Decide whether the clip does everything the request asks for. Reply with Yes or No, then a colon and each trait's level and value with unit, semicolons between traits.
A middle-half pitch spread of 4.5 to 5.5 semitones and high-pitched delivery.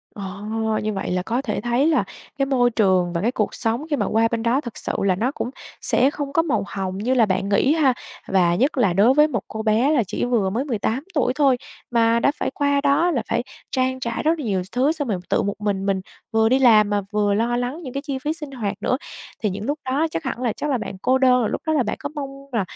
Yes: average, 4.9 semitones; high, 240 Hz